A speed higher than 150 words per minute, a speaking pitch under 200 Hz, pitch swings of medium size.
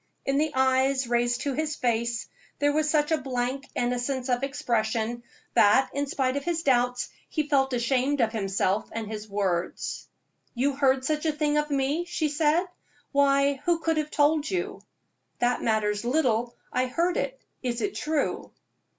No: average, 165 wpm; very high, 270 Hz; average, 3.7 semitones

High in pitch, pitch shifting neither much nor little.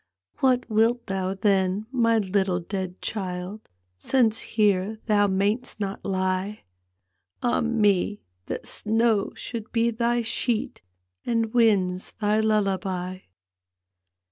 Yes: high, 210 Hz; average, 3.2 semitones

